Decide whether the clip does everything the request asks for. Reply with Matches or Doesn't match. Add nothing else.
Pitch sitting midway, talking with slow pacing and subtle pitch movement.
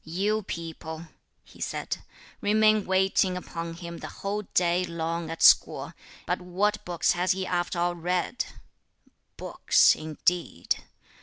Matches